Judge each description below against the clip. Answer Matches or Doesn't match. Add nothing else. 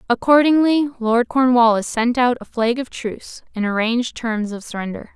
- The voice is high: Matches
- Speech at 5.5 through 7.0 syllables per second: Doesn't match